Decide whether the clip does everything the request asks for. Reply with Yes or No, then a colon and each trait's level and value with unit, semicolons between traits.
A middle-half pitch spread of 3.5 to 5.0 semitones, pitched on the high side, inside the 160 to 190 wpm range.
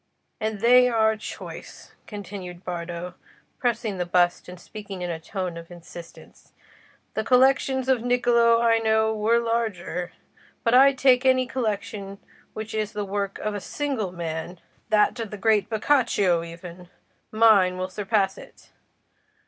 No: average, 4.4 semitones; high, 210 Hz; slow, 135 wpm